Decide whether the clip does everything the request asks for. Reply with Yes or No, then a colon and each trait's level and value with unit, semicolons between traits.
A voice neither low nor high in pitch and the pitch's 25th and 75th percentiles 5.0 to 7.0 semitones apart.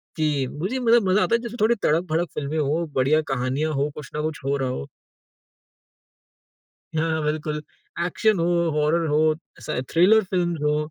No: medium, 155 Hz; average, 3.2 semitones